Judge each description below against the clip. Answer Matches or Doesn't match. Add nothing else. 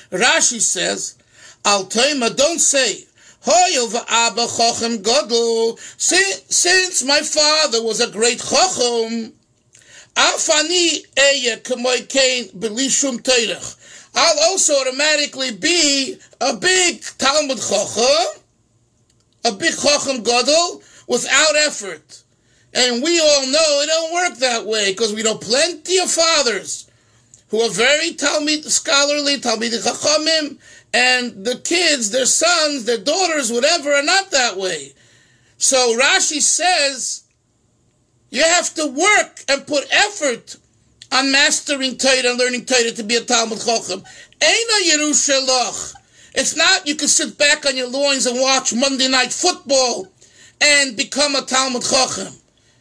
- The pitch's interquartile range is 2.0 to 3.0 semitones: Doesn't match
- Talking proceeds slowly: Matches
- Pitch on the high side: Matches